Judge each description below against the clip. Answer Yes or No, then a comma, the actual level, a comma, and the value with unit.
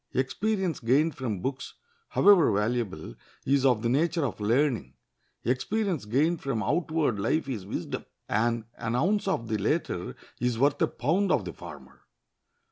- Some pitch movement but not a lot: No, wide, 6.2 semitones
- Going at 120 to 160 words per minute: Yes, average, 150 wpm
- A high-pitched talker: No, low, 130 Hz